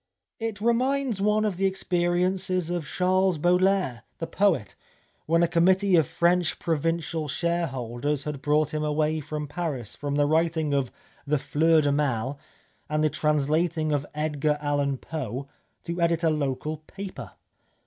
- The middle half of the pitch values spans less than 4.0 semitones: Yes, average, 3.4 semitones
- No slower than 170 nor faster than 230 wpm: No, average, 150 wpm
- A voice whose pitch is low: No, medium, 155 Hz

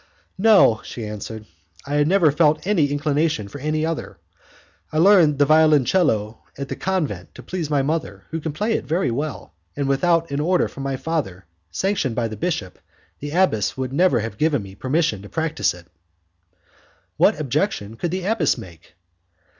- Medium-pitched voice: Yes, medium, 150 Hz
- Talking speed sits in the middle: Yes, average, 170 wpm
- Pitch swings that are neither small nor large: No, wide, 6.1 semitones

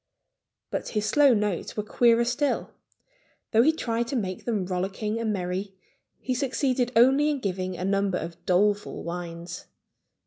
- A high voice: Yes, high, 210 Hz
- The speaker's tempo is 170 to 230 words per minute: No, average, 150 wpm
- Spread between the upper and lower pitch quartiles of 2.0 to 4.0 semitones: No, average, 4.7 semitones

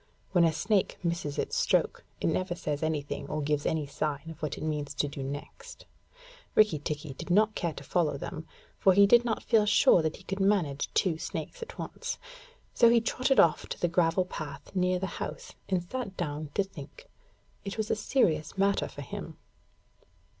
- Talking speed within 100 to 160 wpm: No, average, 195 wpm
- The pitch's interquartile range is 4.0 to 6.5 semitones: Yes, average, 4.9 semitones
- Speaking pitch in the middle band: Yes, medium, 170 Hz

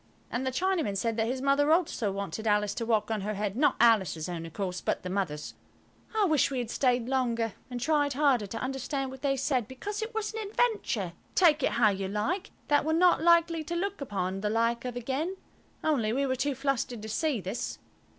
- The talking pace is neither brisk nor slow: No, fast, 215 wpm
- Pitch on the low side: No, very high, 255 Hz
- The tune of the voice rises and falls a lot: Yes, wide, 6.1 semitones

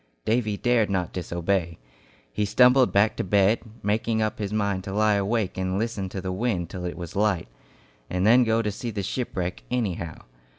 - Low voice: Yes, low, 100 Hz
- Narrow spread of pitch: No, average, 3.1 semitones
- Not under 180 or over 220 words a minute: Yes, average, 185 wpm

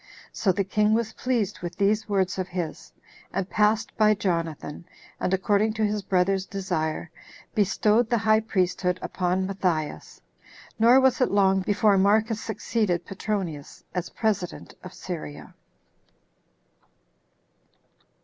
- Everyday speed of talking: No, slow, 125 wpm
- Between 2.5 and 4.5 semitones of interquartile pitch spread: Yes, average, 3.1 semitones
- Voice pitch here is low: No, high, 195 Hz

